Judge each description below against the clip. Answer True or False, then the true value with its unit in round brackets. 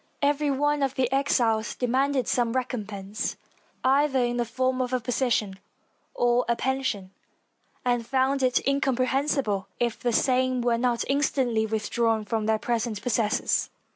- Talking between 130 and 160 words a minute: True (140 wpm)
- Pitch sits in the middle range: False (245 Hz)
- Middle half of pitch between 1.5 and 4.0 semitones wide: True (2.7 semitones)